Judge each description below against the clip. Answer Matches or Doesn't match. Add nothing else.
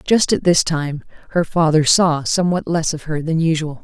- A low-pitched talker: Doesn't match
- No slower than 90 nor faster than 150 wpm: Doesn't match